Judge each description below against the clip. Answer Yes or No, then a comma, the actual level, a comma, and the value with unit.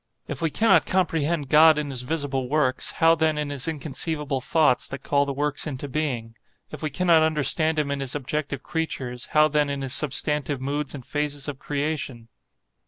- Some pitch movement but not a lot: No, narrow, 2.2 semitones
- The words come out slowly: No, average, 185 wpm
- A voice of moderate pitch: Yes, medium, 145 Hz